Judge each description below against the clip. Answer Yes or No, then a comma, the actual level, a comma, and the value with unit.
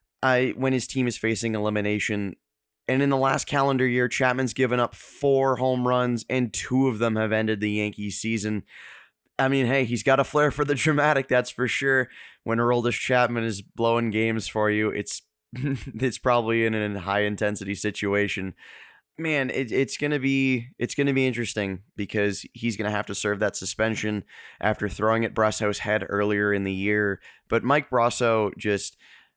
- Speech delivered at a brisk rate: No, average, 180 wpm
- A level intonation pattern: No, average, 3.7 semitones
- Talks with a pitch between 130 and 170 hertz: No, low, 115 Hz